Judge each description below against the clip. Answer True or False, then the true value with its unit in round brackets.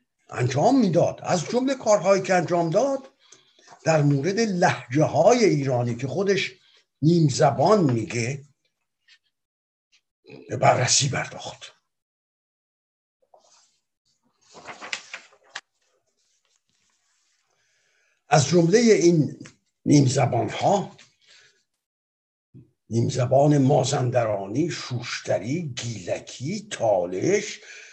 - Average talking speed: False (70 wpm)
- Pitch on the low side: False (150 Hz)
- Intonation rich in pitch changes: True (7.0 semitones)